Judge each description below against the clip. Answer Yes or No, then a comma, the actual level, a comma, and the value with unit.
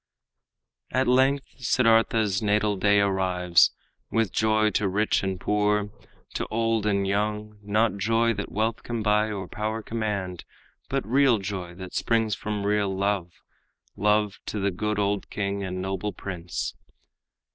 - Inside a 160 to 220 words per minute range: No, average, 145 wpm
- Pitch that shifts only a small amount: Yes, narrow, 1.9 semitones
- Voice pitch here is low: Yes, low, 105 Hz